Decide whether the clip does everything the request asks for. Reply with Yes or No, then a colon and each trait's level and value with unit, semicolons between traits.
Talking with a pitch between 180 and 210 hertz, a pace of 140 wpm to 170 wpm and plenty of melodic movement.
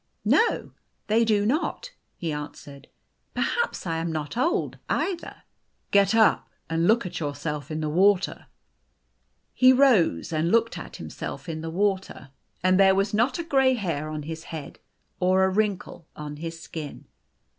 Yes: medium, 185 Hz; average, 160 wpm; wide, 5.8 semitones